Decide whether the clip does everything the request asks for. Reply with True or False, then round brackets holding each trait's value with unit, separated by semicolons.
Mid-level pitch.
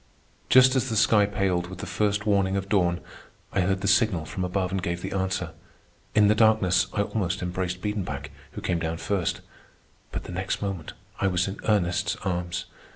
False (95 Hz)